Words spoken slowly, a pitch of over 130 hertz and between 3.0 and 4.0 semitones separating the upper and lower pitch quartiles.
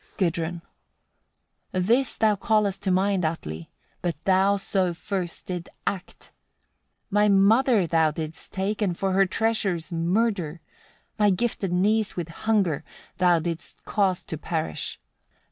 Yes: slow, 130 wpm; high, 190 Hz; average, 3.3 semitones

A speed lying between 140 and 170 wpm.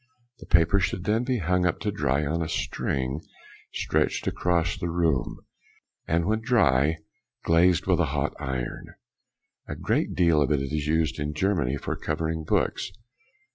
Yes: average, 160 wpm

